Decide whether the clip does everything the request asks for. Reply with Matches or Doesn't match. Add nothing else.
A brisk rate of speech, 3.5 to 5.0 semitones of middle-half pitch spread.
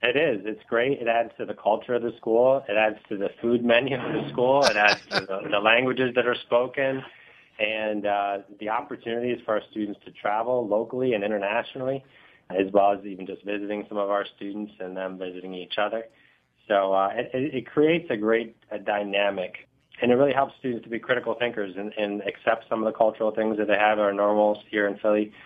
Doesn't match